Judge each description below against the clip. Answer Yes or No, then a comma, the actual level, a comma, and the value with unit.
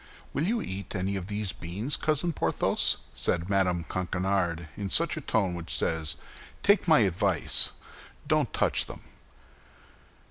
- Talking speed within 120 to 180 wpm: Yes, slow, 135 wpm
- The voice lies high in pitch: No, very low, 95 Hz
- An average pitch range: Yes, average, 4.8 semitones